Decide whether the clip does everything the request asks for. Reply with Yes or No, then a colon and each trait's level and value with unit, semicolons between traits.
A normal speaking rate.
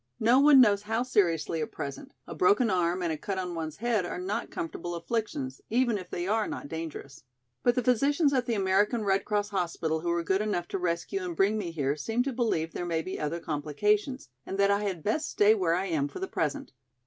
No: fast, 230 wpm